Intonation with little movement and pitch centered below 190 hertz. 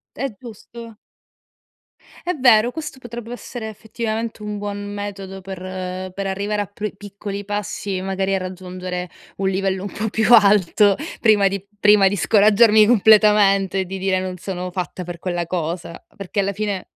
No: narrow, 2.3 semitones; high, 200 Hz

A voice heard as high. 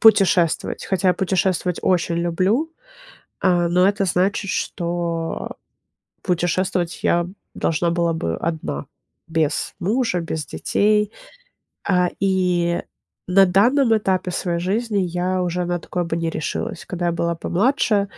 No: medium, 180 Hz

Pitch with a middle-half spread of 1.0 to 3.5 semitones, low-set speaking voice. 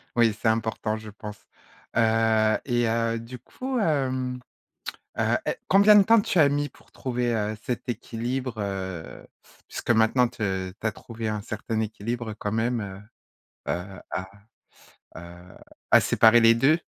Yes: average, 2.7 semitones; low, 115 Hz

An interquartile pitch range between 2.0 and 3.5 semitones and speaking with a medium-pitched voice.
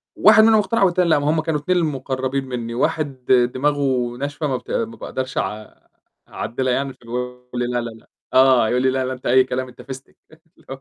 No: average, 3.0 semitones; low, 130 Hz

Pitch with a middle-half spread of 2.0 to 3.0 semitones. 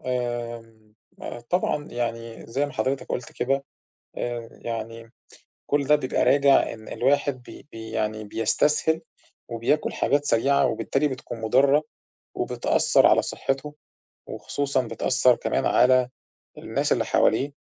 No: average, 3.4 semitones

